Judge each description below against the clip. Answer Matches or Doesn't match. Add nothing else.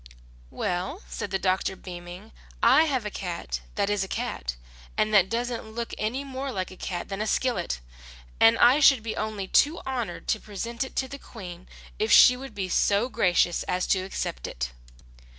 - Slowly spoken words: Doesn't match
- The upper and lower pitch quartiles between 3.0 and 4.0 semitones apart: Doesn't match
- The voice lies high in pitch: Matches